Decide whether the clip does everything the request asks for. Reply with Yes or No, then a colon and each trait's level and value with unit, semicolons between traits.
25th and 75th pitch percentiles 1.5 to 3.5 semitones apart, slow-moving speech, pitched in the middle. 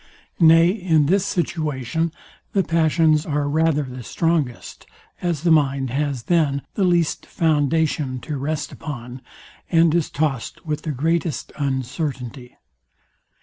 Yes: average, 3.1 semitones; slow, 125 wpm; medium, 155 Hz